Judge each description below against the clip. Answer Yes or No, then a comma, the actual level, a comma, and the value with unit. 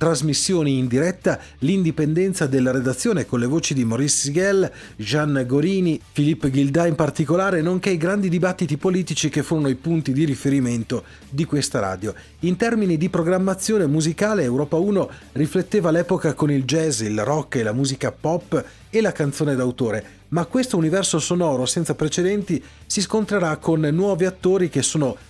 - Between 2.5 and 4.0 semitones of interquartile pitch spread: No, average, 4.8 semitones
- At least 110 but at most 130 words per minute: No, average, 155 wpm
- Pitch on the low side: No, medium, 160 Hz